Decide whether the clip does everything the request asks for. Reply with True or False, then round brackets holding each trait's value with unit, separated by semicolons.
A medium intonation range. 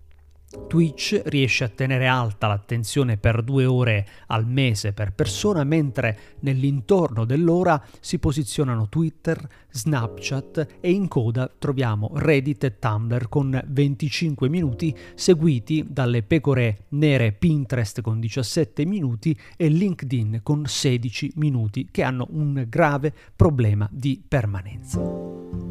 True (4.9 semitones)